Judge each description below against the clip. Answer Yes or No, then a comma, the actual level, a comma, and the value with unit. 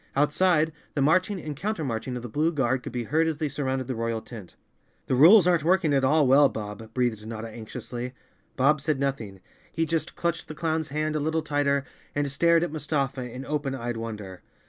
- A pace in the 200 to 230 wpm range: Yes, fast, 205 wpm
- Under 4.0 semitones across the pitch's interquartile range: No, average, 4.3 semitones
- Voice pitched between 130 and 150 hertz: Yes, medium, 140 Hz